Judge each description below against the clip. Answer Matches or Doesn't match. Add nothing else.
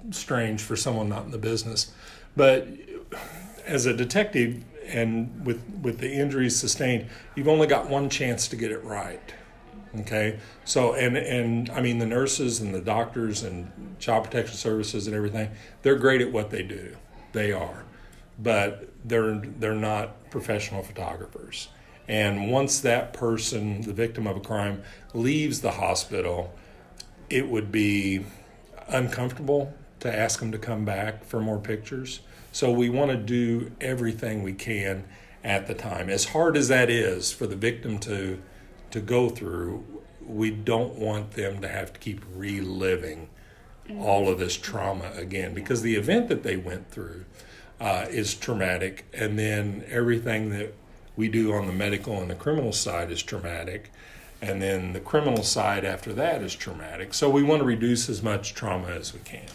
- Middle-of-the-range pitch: Doesn't match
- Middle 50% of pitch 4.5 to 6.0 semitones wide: Doesn't match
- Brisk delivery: Doesn't match